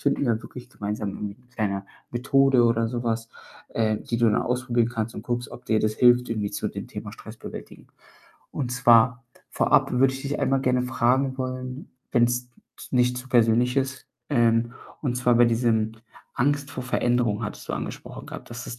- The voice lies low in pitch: Yes, low, 120 Hz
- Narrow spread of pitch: Yes, narrow, 1.9 semitones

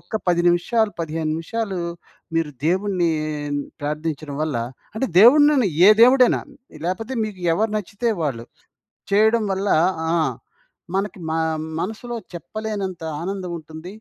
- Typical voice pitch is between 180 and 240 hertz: Yes, high, 190 Hz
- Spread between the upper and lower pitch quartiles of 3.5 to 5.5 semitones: Yes, average, 5.0 semitones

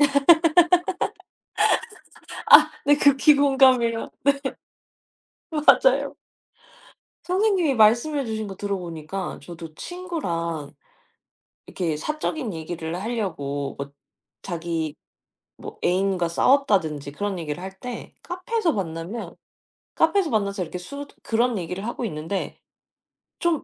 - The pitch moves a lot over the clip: Yes, wide, 8.8 semitones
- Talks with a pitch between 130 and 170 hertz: No, high, 200 Hz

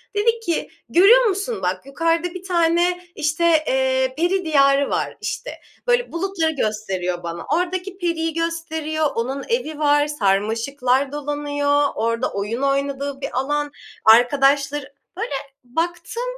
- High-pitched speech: Yes, very high, 295 Hz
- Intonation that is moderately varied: Yes, average, 4.3 semitones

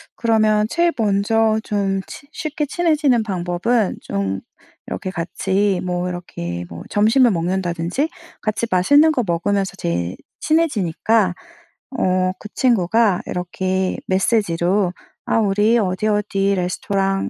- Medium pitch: No, high, 195 Hz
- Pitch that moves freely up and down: No, average, 3.9 semitones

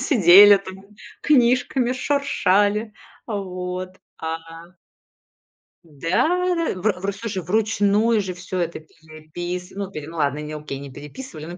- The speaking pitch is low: No, medium, 185 Hz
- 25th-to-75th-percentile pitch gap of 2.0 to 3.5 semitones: No, average, 4.4 semitones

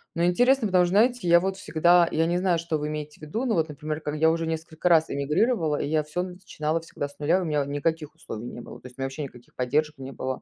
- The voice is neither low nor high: Yes, medium, 160 Hz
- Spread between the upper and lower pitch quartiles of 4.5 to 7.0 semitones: No, average, 3.0 semitones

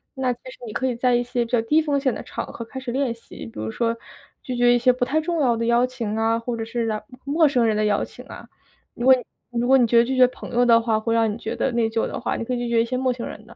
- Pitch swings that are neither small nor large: No, narrow, 1.9 semitones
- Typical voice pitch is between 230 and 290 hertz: Yes, high, 240 Hz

